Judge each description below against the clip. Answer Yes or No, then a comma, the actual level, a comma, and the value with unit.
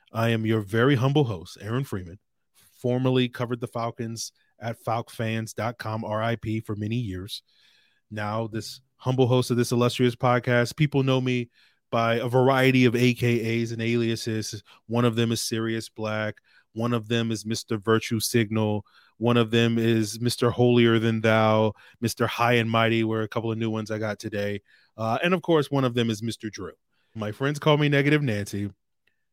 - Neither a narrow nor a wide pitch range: No, narrow, 1.9 semitones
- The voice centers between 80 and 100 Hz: No, low, 115 Hz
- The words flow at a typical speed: Yes, average, 175 wpm